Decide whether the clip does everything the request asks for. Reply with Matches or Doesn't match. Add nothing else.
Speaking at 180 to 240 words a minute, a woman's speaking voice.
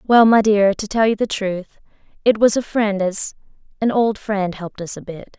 Matches